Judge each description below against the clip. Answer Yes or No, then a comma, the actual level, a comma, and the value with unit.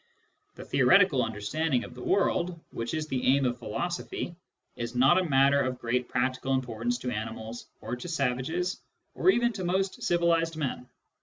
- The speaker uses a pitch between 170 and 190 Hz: No, low, 135 Hz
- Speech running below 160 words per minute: No, average, 165 wpm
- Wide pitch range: Yes, wide, 5.7 semitones